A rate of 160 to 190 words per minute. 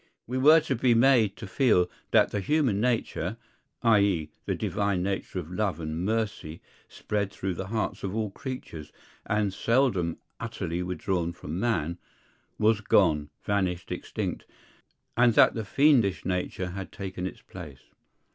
No: average, 145 wpm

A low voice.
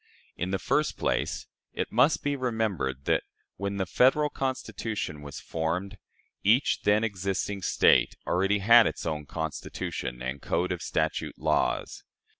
Yes: low, 100 Hz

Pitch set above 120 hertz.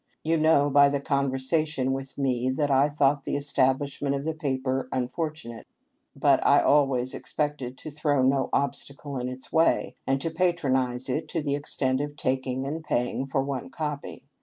Yes: medium, 140 Hz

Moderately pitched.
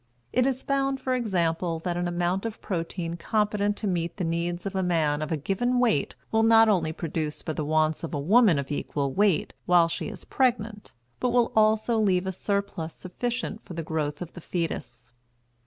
Yes: medium, 180 Hz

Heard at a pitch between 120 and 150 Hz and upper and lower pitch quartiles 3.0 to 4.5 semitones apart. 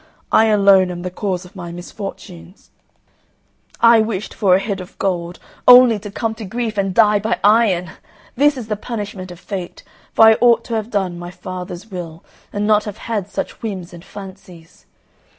No: high, 200 Hz; average, 3.4 semitones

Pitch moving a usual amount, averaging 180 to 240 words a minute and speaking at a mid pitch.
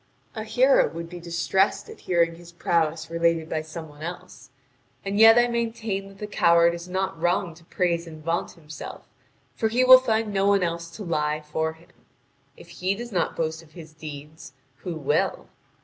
Yes: average, 3.6 semitones; average, 190 wpm; medium, 170 Hz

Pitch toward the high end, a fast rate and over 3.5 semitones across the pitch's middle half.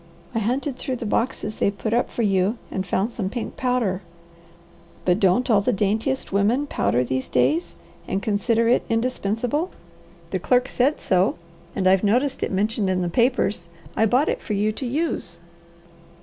No: high, 215 Hz; average, 180 wpm; average, 4.7 semitones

